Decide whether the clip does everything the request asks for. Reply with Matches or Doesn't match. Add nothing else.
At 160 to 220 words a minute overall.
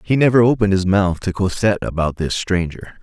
Matches